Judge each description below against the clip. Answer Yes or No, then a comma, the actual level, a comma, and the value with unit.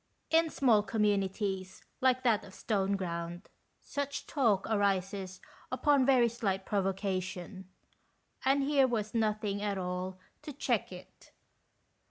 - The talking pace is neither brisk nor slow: No, slow, 115 wpm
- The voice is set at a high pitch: Yes, high, 205 Hz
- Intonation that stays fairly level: No, average, 4.3 semitones